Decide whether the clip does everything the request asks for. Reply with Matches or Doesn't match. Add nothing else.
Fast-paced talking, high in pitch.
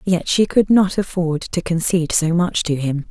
Doesn't match